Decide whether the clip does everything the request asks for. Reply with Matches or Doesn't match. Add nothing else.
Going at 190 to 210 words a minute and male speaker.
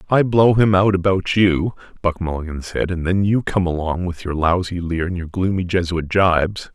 Matches